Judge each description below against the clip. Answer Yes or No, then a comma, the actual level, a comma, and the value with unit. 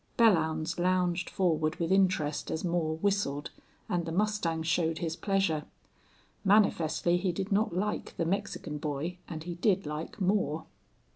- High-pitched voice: No, medium, 175 Hz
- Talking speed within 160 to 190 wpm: No, average, 145 wpm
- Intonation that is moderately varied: Yes, average, 3.3 semitones